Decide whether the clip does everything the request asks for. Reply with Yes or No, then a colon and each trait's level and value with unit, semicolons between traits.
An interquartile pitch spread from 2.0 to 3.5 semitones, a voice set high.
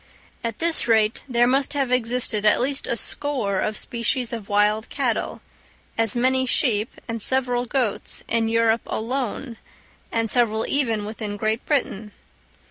Yes: average, 2.7 semitones; high, 230 Hz